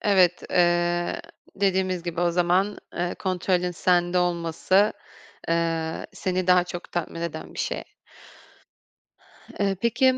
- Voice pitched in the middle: Yes, medium, 175 Hz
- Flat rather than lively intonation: Yes, narrow, 1.3 semitones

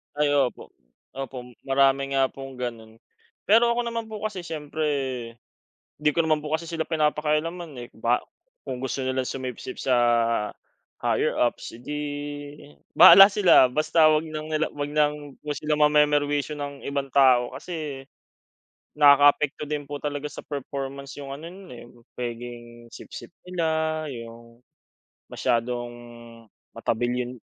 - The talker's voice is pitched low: No, medium, 145 Hz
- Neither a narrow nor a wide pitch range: Yes, average, 3.1 semitones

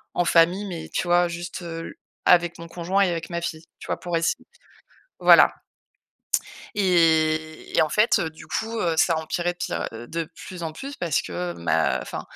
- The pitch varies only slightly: Yes, narrow, 1.8 semitones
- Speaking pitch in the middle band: Yes, medium, 170 Hz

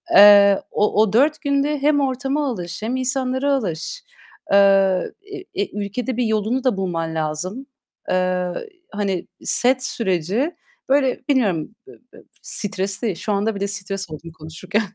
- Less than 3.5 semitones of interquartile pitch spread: No, wide, 5.6 semitones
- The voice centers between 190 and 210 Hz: Yes, high, 205 Hz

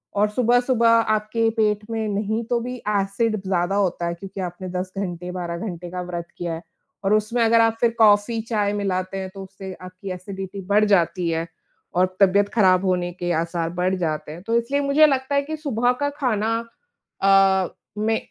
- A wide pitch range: No, average, 3.8 semitones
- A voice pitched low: No, high, 200 Hz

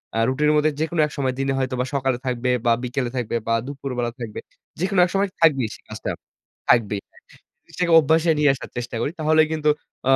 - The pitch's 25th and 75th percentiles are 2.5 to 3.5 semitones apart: No, average, 4.2 semitones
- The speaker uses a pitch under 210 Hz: Yes, low, 135 Hz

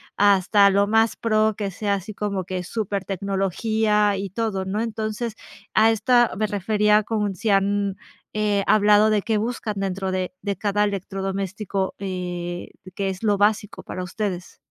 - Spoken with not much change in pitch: Yes, narrow, 1.9 semitones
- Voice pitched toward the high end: Yes, high, 205 Hz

